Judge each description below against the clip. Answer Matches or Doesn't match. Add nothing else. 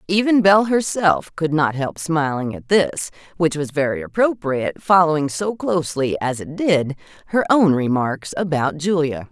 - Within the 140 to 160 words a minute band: Matches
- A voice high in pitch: Doesn't match